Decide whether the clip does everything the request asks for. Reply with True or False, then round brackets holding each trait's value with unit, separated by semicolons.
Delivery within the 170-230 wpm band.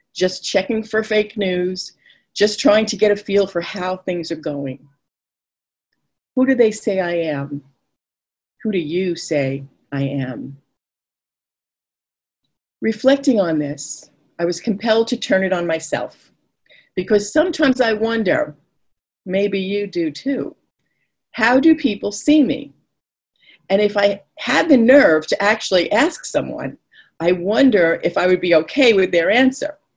False (145 wpm)